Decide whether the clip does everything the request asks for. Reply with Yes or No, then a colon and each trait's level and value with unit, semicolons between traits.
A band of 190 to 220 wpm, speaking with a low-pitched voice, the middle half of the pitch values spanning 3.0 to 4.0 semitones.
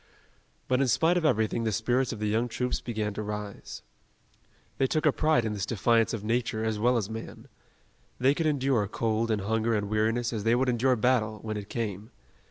No: fast, 205 wpm; low, 115 Hz; narrow, 2.6 semitones